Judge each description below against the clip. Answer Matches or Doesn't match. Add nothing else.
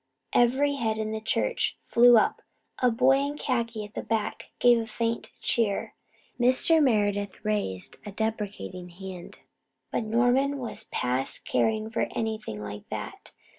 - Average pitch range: Matches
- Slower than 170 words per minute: Matches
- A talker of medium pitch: Doesn't match